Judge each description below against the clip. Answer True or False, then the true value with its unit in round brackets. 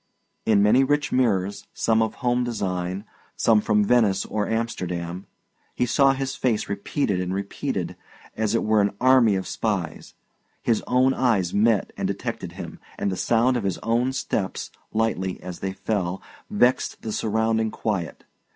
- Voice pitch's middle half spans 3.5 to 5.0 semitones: True (3.9 semitones)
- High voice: False (110 Hz)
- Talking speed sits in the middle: True (160 wpm)